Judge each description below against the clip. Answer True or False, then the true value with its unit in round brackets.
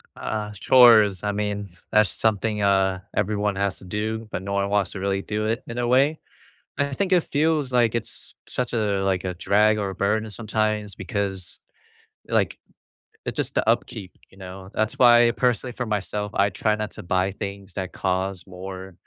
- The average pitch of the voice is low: True (105 Hz)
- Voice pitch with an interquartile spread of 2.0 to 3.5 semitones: True (2.4 semitones)